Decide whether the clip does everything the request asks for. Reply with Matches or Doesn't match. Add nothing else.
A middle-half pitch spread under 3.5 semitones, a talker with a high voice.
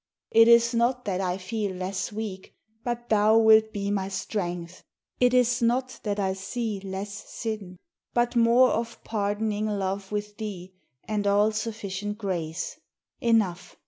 Matches